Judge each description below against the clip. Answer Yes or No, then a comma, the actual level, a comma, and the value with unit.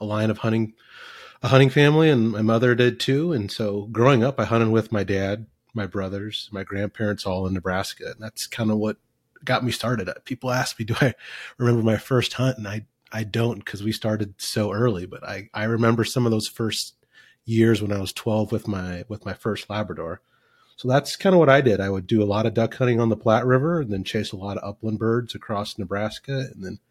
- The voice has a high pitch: No, low, 110 Hz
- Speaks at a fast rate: Yes, fast, 230 wpm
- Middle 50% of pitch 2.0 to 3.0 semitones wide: Yes, average, 2.7 semitones